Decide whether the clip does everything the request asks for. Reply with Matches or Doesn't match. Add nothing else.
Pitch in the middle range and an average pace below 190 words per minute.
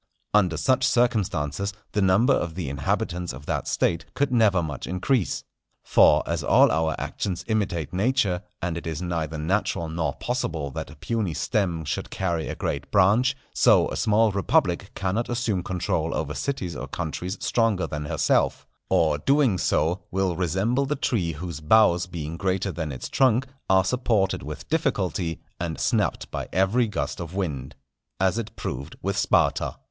Doesn't match